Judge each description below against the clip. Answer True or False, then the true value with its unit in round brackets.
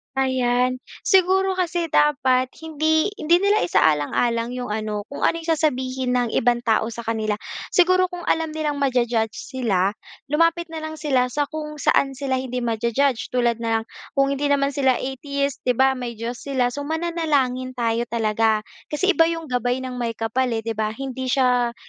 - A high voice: True (260 Hz)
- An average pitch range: True (4.2 semitones)